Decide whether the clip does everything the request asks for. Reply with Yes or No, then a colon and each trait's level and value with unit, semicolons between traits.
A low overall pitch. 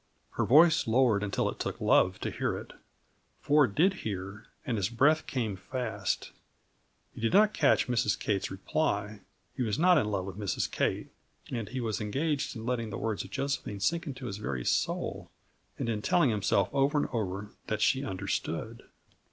Yes: low, 115 Hz